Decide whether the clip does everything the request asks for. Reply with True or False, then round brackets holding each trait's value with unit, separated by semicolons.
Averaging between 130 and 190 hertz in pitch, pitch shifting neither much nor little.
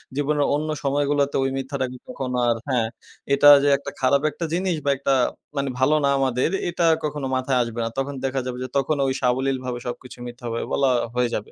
False (135 Hz; 2.0 semitones)